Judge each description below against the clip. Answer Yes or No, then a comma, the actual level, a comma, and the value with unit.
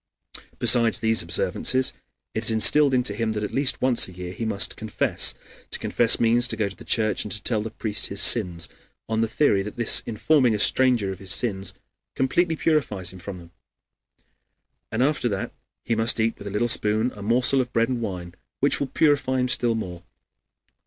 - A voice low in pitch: Yes, low, 110 Hz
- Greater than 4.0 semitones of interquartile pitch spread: No, average, 3.7 semitones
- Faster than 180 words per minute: Yes, average, 200 wpm